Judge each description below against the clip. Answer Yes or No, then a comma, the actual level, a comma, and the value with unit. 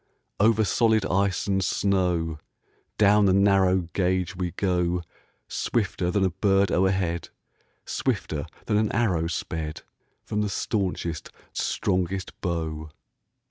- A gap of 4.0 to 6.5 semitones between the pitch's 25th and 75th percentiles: No, narrow, 2.4 semitones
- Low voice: Yes, very low, 95 Hz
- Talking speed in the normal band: No, slow, 115 wpm